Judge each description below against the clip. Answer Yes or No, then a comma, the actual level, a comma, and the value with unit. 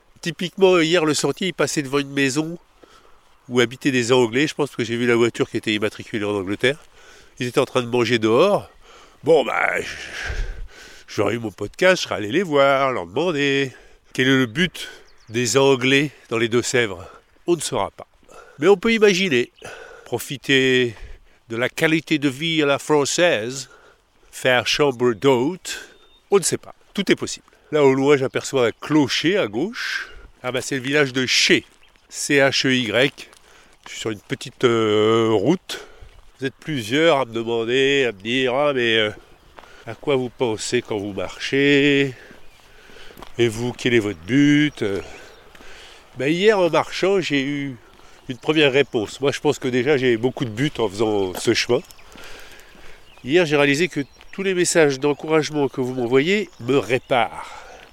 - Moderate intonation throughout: Yes, average, 3.7 semitones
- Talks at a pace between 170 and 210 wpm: Yes, average, 175 wpm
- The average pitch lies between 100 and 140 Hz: Yes, low, 135 Hz